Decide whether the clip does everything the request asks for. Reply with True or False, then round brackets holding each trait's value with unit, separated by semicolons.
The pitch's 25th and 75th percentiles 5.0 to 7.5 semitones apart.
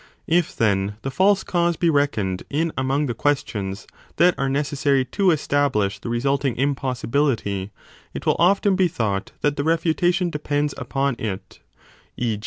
True (5.6 semitones)